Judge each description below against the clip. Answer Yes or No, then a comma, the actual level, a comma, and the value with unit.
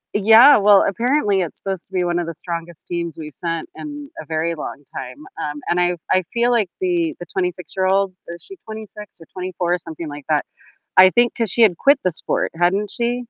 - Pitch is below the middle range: No, medium, 185 Hz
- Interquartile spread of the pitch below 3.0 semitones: No, average, 4.7 semitones